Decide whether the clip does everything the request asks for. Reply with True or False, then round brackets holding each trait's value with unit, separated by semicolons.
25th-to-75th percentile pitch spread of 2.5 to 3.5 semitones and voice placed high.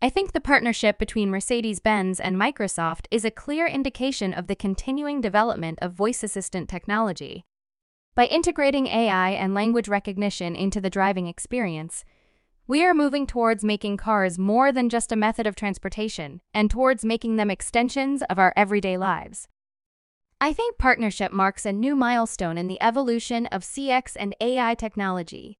False (4.0 semitones; 215 Hz)